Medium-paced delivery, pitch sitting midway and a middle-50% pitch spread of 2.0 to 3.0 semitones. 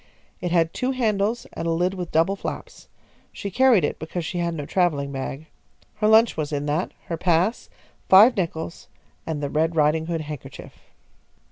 No: average, 170 wpm; medium, 170 Hz; average, 3.9 semitones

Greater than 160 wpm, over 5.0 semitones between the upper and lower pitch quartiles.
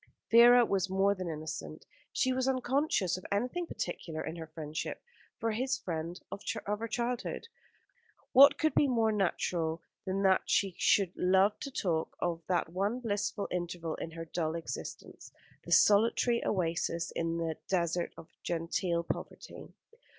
No: average, 150 wpm; wide, 5.5 semitones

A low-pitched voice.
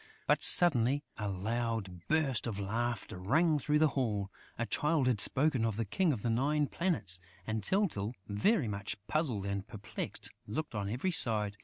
Yes: low, 115 Hz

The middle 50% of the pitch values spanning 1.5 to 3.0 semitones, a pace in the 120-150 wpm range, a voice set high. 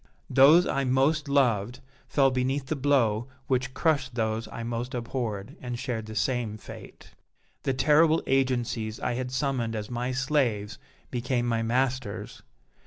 No: average, 2.7 semitones; average, 145 wpm; low, 125 Hz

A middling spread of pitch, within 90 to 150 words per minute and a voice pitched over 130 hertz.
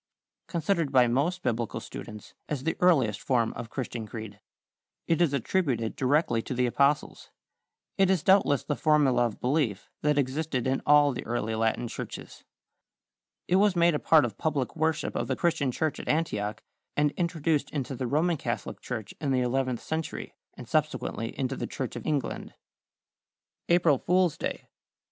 No: average, 4.9 semitones; average, 165 wpm; medium, 140 Hz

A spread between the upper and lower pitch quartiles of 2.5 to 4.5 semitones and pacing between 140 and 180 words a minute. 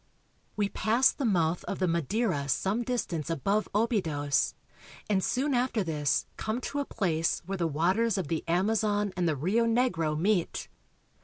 No: wide, 5.4 semitones; average, 160 wpm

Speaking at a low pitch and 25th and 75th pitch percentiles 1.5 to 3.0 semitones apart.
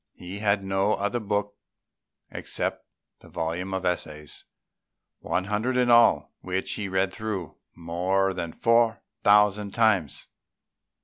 Yes: low, 100 Hz; narrow, 2.4 semitones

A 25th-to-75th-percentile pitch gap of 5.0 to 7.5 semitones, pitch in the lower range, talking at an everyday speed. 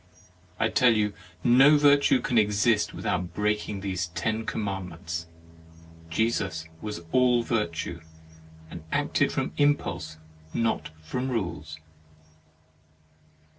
No: wide, 5.5 semitones; low, 105 Hz; slow, 110 wpm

